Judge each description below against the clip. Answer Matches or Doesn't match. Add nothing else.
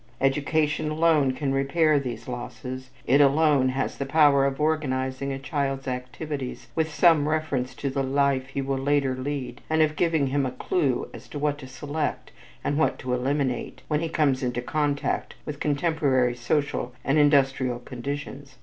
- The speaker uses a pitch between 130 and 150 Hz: Matches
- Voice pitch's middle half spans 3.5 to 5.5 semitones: Doesn't match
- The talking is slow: Doesn't match